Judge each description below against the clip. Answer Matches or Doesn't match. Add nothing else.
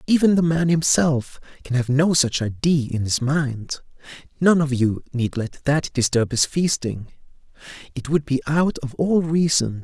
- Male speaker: Matches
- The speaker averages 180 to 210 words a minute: Doesn't match